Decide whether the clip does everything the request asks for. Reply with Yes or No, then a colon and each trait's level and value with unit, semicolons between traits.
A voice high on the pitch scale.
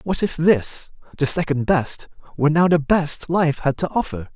No: medium, 155 Hz